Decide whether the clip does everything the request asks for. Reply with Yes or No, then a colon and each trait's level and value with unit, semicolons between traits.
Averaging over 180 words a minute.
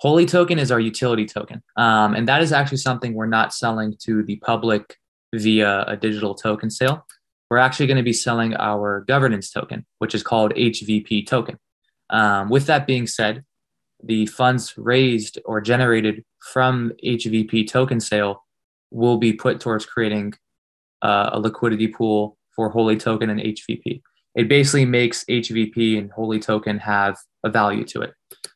No: average, 160 wpm